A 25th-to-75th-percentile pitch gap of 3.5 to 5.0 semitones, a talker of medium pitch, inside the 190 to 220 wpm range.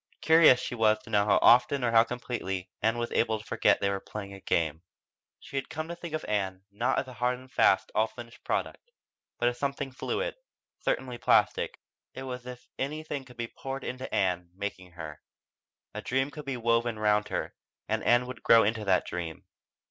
No: average, 4.0 semitones; low, 120 Hz; fast, 205 wpm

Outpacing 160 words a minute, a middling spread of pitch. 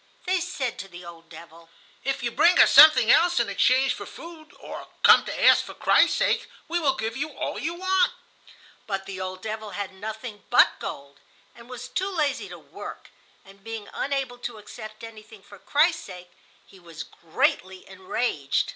No: average, 180 wpm; wide, 6.8 semitones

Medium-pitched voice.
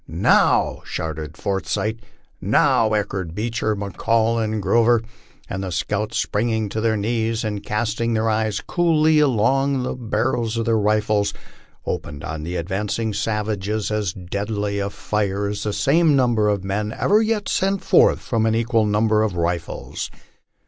No: low, 110 Hz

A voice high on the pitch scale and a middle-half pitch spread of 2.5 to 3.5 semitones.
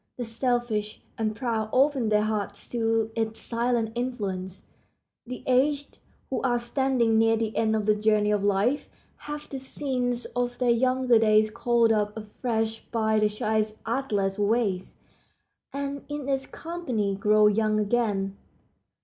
Yes: high, 225 Hz; average, 2.8 semitones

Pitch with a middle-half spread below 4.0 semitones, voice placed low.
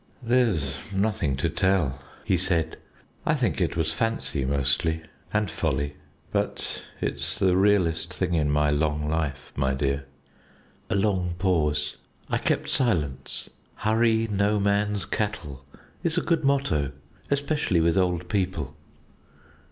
No: wide, 5.6 semitones; very low, 90 Hz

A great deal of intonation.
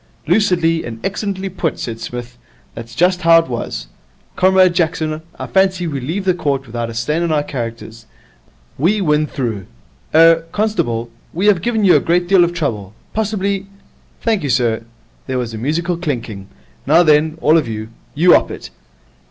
Yes: wide, 7.1 semitones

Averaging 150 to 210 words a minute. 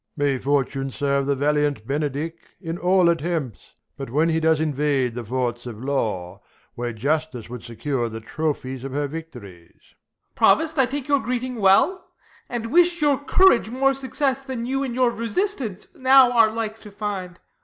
Yes: average, 175 wpm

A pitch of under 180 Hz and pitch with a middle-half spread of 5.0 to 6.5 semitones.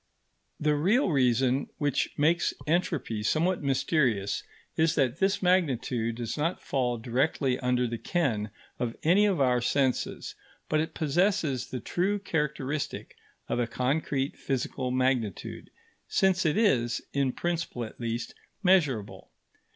Yes: medium, 140 Hz; average, 5.3 semitones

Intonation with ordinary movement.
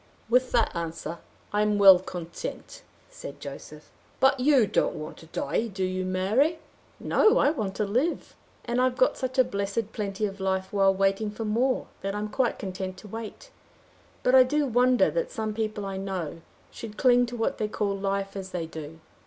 Yes: average, 4.5 semitones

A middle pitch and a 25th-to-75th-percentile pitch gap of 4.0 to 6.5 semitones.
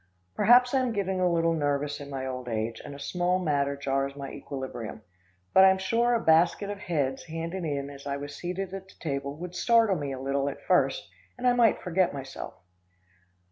Yes: medium, 160 Hz; average, 5.3 semitones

